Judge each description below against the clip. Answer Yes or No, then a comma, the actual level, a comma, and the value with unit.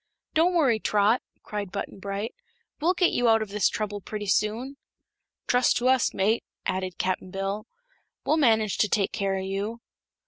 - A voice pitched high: Yes, high, 210 Hz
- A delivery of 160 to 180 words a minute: Yes, average, 170 wpm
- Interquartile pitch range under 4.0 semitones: Yes, average, 3.5 semitones